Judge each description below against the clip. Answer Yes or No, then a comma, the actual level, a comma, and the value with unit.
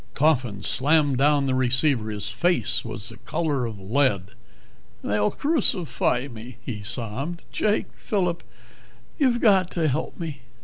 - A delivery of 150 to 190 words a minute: No, slow, 135 wpm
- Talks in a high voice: No, low, 135 Hz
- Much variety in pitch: Yes, wide, 6.6 semitones